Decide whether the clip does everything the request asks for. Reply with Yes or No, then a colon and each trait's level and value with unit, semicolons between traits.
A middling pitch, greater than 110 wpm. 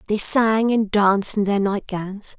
No: high, 205 Hz; average, 200 wpm